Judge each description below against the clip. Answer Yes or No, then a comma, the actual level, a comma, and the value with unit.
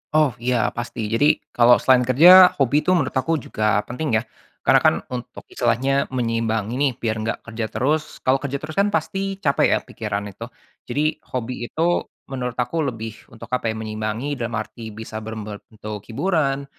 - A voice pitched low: Yes, low, 125 Hz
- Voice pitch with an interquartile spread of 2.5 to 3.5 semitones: No, average, 4.1 semitones